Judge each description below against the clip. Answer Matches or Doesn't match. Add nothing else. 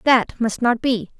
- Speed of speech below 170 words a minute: Doesn't match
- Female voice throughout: Matches